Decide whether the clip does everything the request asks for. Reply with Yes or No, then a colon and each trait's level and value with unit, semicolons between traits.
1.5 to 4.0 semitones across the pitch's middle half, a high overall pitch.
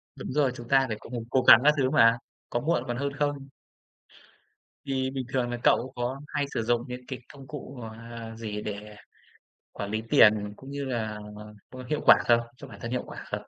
No: average, 2.8 semitones; low, 125 Hz